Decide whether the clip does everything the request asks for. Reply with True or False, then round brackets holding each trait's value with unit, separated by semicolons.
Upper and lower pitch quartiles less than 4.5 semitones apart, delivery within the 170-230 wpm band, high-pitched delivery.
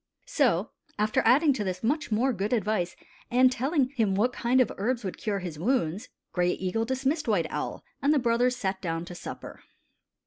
False (5.2 semitones; 185 wpm; 225 Hz)